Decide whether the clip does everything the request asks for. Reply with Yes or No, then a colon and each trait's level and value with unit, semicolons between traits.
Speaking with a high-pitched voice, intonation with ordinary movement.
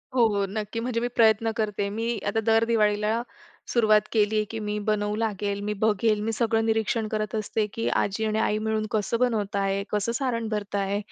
No: high, 215 Hz; narrow, 1.5 semitones